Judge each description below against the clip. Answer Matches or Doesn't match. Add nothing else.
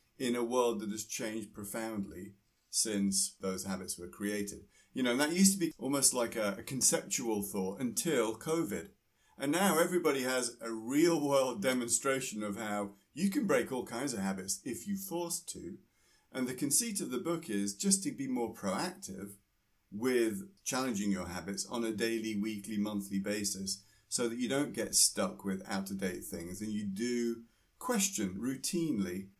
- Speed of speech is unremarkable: Matches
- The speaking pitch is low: Matches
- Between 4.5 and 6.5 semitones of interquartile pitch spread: Matches